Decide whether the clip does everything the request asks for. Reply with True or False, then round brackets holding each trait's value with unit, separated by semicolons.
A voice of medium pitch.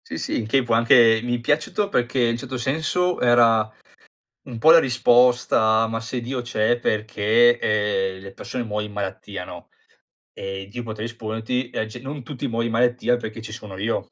False (115 Hz)